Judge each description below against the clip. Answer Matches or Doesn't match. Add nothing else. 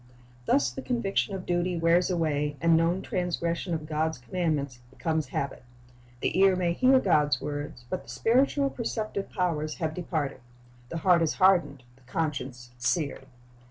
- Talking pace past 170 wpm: Doesn't match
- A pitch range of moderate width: Matches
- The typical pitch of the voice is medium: Matches